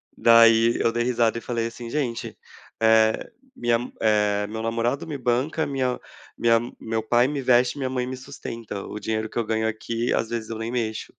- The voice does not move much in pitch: Yes, narrow, 1.7 semitones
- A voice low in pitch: Yes, low, 115 Hz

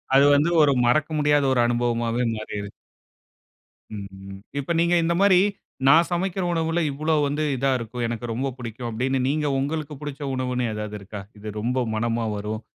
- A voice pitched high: No, low, 125 Hz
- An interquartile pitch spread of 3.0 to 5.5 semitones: Yes, average, 4.7 semitones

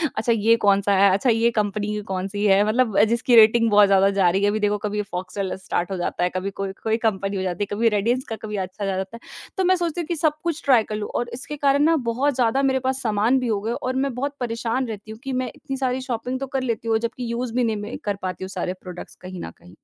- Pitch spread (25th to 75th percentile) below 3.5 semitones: No, average, 4.2 semitones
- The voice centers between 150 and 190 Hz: No, high, 220 Hz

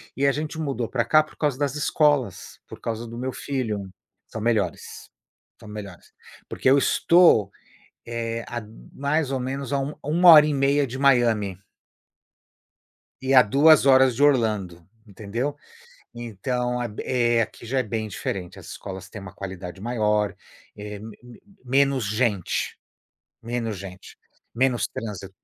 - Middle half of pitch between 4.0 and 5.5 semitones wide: Yes, average, 4.6 semitones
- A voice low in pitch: Yes, low, 120 Hz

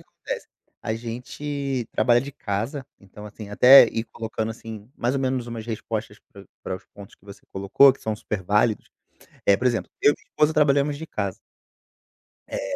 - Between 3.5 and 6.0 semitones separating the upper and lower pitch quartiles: Yes, average, 4.5 semitones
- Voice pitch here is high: No, low, 115 Hz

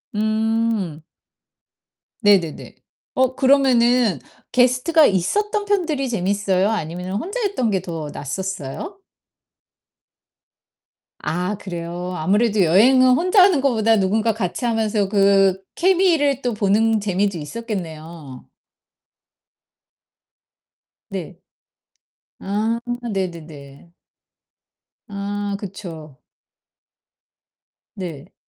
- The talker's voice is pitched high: Yes, high, 205 Hz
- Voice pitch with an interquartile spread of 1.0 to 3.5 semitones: No, wide, 5.5 semitones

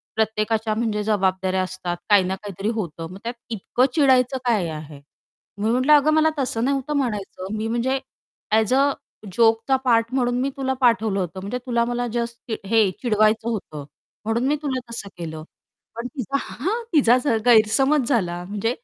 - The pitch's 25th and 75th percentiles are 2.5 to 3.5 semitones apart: No, average, 4.1 semitones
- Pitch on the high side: Yes, high, 225 Hz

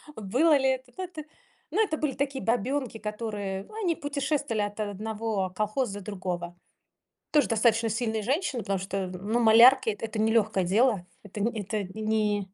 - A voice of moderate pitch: No, high, 220 Hz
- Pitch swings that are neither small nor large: Yes, average, 4.3 semitones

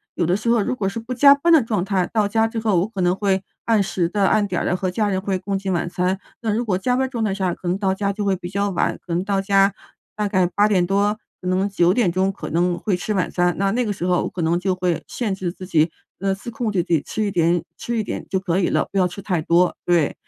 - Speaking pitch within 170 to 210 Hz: Yes, high, 195 Hz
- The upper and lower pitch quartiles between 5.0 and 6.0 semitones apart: No, average, 2.8 semitones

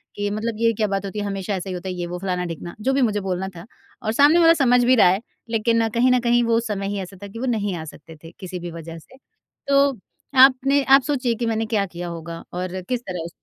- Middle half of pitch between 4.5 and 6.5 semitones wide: Yes, average, 5.0 semitones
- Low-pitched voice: No, high, 205 Hz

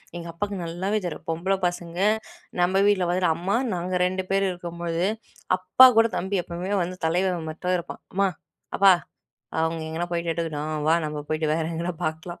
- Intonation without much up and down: Yes, narrow, 2.1 semitones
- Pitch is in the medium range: Yes, medium, 175 Hz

